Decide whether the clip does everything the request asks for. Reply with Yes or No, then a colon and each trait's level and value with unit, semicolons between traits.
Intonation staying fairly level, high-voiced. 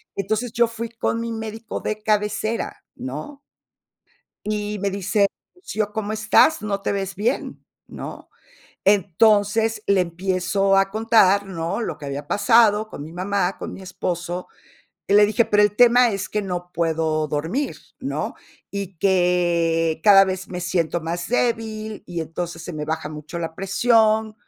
No: average, 3.8 semitones; high, 200 Hz